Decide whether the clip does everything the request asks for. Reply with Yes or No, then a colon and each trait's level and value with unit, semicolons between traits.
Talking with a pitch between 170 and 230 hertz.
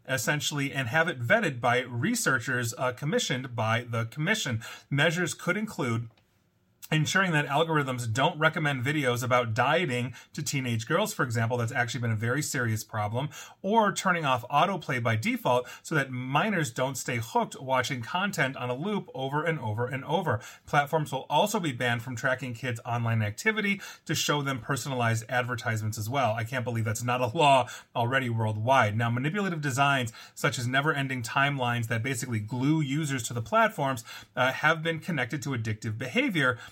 No: low, 130 Hz